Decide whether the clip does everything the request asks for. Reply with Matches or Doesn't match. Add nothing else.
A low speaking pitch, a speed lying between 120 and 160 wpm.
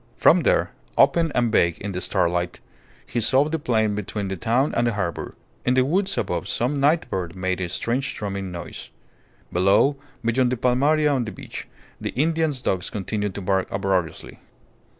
Doesn't match